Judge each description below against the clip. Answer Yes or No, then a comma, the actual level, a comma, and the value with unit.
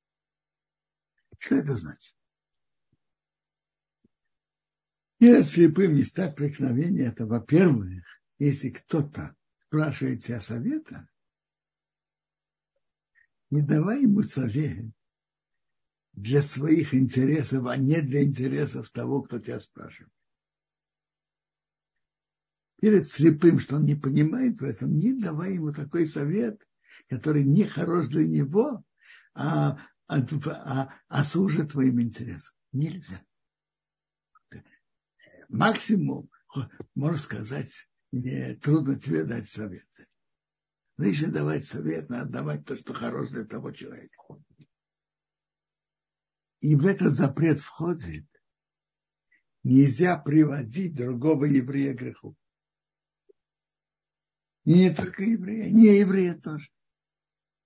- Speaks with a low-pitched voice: No, medium, 145 Hz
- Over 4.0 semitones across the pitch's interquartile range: Yes, average, 4.9 semitones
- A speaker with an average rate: No, slow, 95 wpm